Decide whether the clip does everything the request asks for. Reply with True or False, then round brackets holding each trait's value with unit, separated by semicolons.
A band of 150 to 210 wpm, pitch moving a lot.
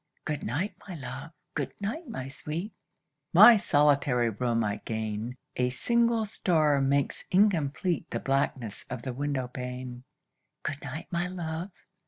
False (140 wpm; 5.7 semitones)